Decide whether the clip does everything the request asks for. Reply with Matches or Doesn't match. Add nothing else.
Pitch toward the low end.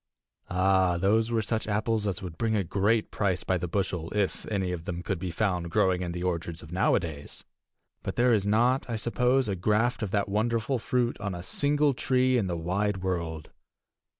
Matches